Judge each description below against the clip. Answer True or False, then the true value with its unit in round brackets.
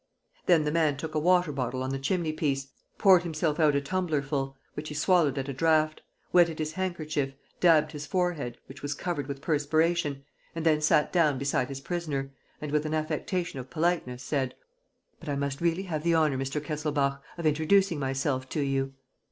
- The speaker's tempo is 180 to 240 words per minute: True (185 wpm)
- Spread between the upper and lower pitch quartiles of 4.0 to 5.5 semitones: False (3.1 semitones)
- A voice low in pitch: False (150 Hz)